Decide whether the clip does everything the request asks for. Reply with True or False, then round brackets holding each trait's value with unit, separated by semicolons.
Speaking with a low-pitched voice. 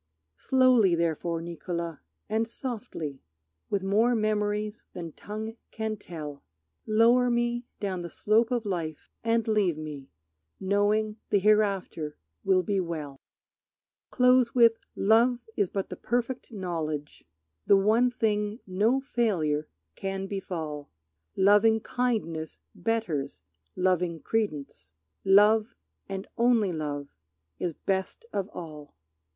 False (200 Hz)